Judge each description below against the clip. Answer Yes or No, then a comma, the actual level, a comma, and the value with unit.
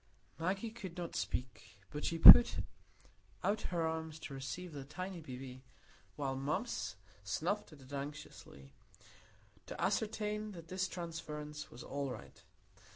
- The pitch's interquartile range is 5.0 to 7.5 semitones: Yes, average, 5.3 semitones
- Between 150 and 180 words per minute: No, slow, 135 wpm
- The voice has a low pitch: No, medium, 155 Hz